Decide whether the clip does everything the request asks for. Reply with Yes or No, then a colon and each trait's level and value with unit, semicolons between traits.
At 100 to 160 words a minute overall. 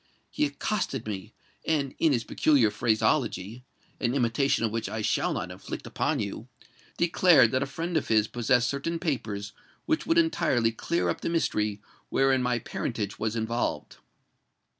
Yes: average, 150 wpm